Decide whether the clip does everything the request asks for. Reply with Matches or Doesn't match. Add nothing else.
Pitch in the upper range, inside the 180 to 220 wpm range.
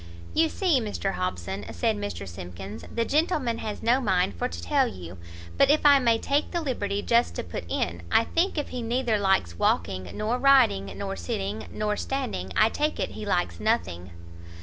Matches